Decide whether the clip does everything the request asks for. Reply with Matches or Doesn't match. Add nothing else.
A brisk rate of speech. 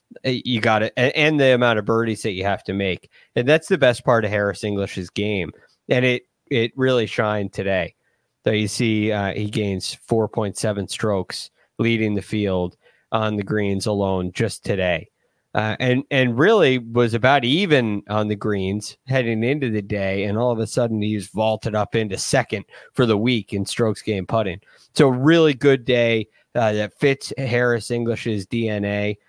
Doesn't match